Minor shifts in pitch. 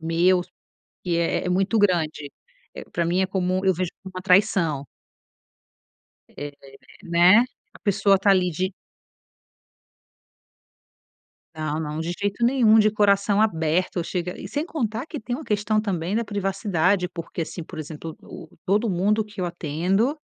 No: average, 3.4 semitones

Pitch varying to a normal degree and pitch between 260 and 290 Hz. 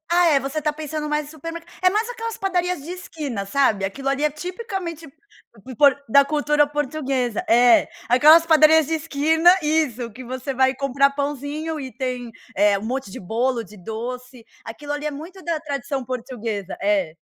Yes: average, 4.1 semitones; very high, 280 Hz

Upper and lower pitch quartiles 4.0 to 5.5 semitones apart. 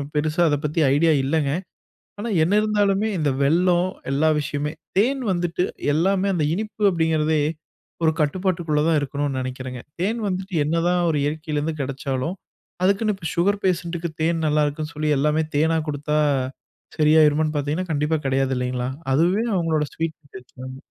No: average, 3.5 semitones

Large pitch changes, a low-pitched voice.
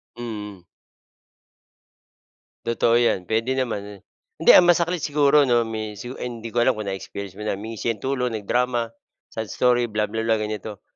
No: average, 2.7 semitones; low, 115 Hz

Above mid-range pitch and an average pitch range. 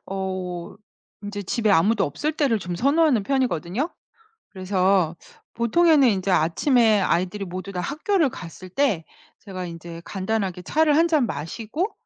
No: high, 200 Hz; wide, 6.8 semitones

